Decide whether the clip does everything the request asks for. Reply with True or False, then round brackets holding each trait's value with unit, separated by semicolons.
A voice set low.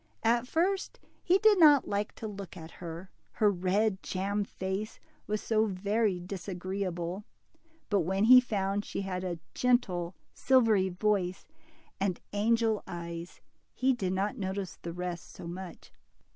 False (195 Hz)